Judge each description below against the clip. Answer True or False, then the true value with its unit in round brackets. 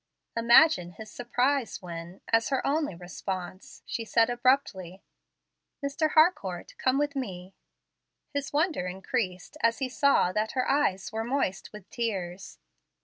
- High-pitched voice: True (230 Hz)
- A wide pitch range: True (6.8 semitones)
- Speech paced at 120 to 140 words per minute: True (135 wpm)